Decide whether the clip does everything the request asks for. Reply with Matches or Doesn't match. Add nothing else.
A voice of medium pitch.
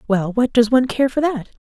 Doesn't match